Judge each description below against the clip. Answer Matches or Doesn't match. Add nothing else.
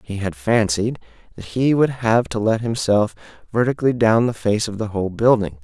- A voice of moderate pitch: Doesn't match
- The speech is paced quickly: Doesn't match